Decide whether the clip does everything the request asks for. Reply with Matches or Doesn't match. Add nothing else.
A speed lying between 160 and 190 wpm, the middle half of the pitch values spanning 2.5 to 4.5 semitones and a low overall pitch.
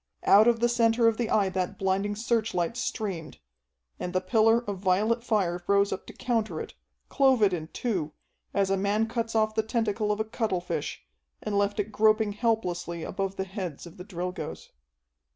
Doesn't match